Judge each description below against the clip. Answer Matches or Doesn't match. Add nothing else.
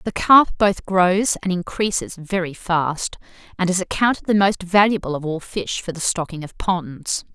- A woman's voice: Matches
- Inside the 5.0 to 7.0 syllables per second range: Doesn't match